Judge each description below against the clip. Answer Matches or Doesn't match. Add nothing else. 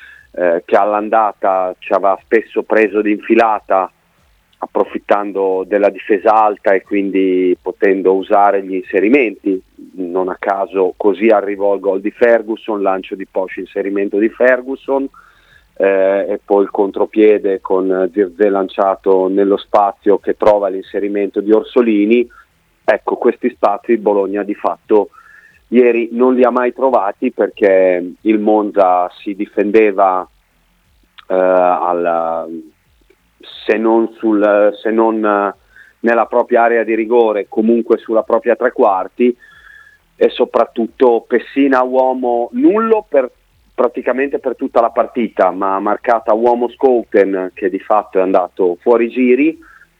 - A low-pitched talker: Matches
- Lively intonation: Doesn't match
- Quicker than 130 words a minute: Doesn't match